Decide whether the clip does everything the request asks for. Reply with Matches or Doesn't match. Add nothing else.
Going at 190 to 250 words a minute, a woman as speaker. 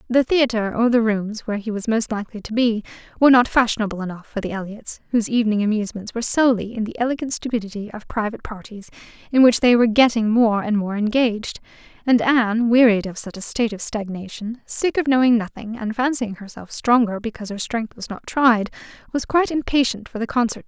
Matches